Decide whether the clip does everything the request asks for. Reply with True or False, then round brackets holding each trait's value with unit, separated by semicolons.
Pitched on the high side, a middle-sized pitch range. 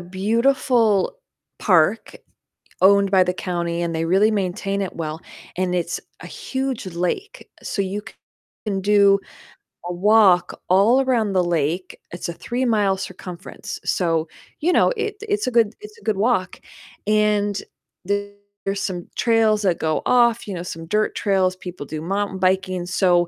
True (195 Hz; 3.2 semitones)